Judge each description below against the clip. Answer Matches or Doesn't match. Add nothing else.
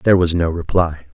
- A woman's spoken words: Doesn't match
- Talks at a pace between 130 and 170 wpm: Doesn't match